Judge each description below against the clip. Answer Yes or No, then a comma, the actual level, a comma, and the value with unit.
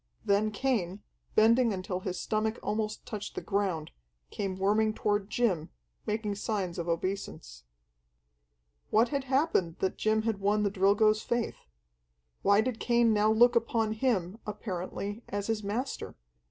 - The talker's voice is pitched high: Yes, high, 210 Hz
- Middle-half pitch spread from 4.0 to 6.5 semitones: No, narrow, 2.5 semitones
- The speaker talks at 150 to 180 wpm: No, average, 140 wpm